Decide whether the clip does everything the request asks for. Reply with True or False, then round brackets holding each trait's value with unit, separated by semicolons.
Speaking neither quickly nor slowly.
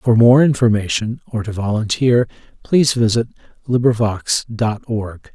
False (125 wpm)